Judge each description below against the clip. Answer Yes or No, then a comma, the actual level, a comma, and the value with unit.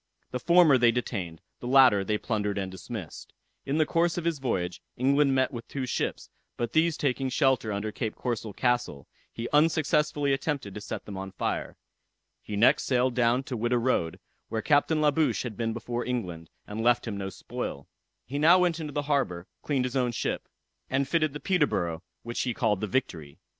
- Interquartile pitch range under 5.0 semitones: No, average, 5.3 semitones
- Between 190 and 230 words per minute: Yes, average, 195 wpm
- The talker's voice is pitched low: Yes, low, 125 Hz